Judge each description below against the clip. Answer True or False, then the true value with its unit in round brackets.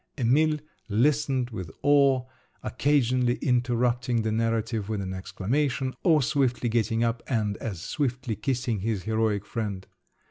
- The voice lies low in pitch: True (120 Hz)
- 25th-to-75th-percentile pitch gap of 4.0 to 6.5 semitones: False (3.2 semitones)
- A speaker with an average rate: False (130 wpm)